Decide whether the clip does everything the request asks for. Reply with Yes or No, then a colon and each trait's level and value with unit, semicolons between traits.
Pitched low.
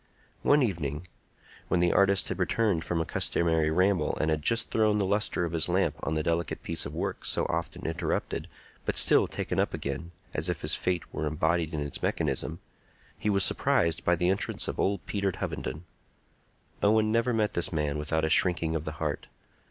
Yes: very low, 85 Hz